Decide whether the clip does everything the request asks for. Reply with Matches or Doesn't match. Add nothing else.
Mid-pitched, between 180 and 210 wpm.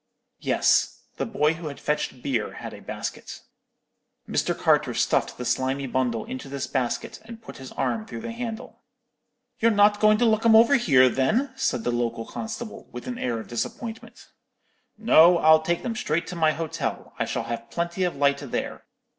Matches